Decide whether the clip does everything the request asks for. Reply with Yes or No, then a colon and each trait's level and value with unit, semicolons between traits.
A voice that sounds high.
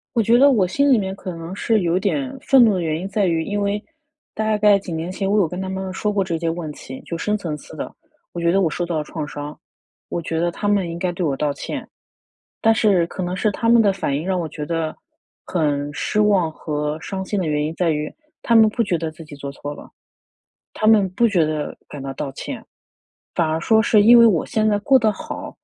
No: medium, 180 Hz